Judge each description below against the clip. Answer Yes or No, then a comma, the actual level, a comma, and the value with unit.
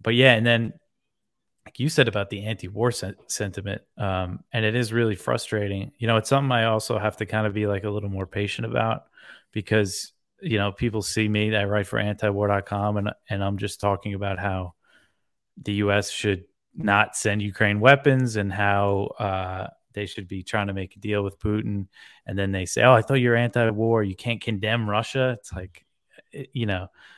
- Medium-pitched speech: No, low, 105 Hz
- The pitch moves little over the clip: Yes, narrow, 2.2 semitones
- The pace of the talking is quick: No, average, 195 wpm